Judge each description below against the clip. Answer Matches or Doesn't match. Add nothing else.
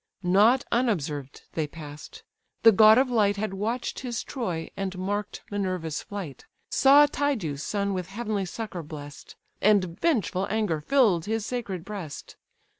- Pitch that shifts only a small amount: Doesn't match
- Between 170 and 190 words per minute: Doesn't match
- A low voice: Doesn't match